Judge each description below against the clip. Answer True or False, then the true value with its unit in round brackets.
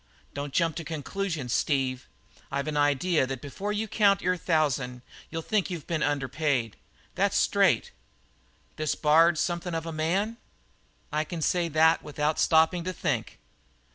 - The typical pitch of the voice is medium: True (160 Hz)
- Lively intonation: False (3.2 semitones)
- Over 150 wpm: True (160 wpm)